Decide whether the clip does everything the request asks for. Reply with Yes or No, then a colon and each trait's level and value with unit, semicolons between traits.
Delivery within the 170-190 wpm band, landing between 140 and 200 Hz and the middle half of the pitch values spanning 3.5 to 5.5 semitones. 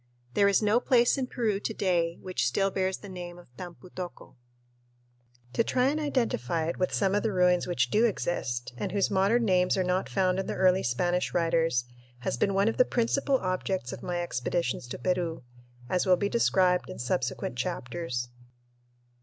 No: average, 185 wpm; medium, 185 Hz; average, 3.1 semitones